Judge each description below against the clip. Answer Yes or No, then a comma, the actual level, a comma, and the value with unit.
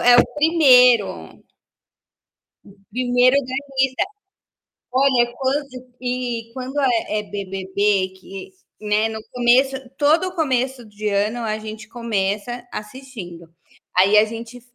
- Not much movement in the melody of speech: No, average, 3.6 semitones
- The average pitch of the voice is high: Yes, high, 240 Hz